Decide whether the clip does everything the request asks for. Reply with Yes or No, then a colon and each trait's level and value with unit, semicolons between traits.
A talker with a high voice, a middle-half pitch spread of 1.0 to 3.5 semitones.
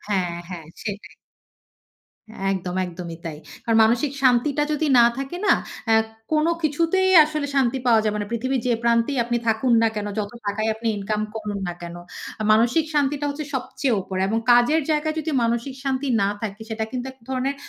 No: high, 235 Hz; average, 4.7 semitones